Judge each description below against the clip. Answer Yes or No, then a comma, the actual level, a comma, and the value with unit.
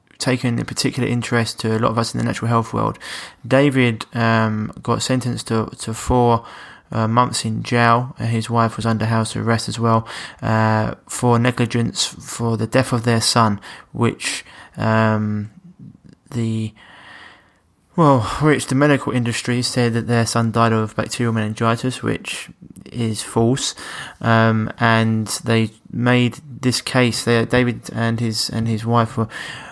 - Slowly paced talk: No, average, 155 wpm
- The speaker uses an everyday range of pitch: No, narrow, 1.6 semitones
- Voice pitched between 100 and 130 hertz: Yes, low, 115 Hz